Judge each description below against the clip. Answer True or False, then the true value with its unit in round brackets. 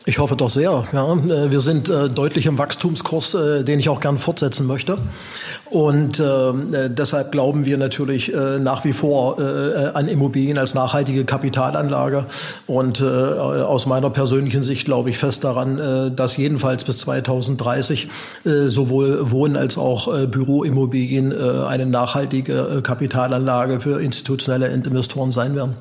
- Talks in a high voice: False (135 Hz)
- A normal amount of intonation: False (1.7 semitones)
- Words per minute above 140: False (130 wpm)